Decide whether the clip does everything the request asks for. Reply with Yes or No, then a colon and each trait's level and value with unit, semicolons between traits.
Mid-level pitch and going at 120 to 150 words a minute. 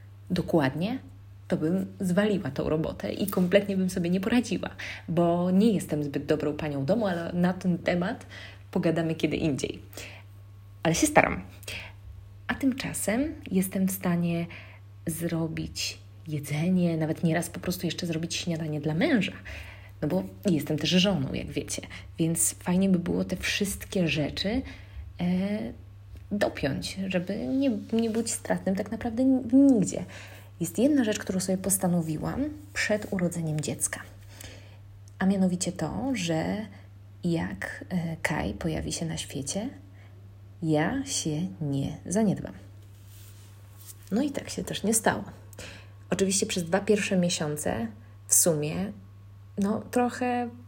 Yes: medium, 160 Hz; average, 130 wpm